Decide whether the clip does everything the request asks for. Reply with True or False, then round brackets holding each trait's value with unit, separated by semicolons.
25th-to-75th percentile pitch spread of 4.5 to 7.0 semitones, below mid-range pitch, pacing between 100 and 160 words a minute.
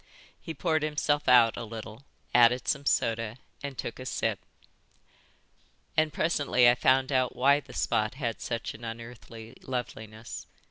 False (3.6 semitones; 125 Hz; 145 wpm)